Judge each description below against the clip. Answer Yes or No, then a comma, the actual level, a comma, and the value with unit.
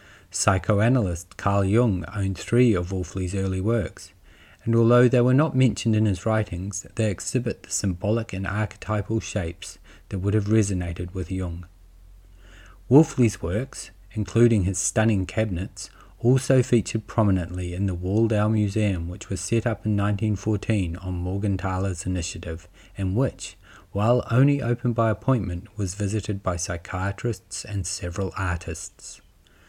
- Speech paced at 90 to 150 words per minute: Yes, slow, 135 wpm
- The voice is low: Yes, low, 100 Hz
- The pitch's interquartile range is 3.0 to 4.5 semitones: Yes, average, 3.4 semitones